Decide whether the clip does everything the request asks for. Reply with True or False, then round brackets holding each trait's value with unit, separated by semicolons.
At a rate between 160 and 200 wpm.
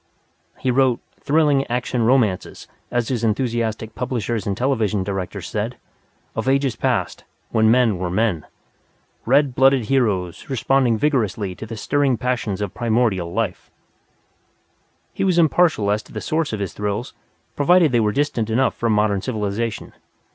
False (145 wpm)